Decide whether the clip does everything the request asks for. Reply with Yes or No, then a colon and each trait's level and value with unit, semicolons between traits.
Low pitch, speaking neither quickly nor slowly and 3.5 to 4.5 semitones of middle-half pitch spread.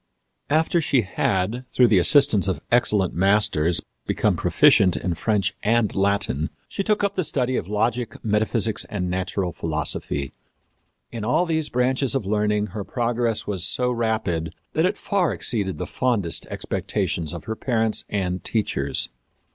No: low, 105 Hz; average, 150 wpm; average, 4.9 semitones